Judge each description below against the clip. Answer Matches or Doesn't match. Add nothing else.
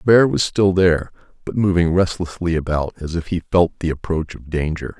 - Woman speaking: Doesn't match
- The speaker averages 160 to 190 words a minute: Doesn't match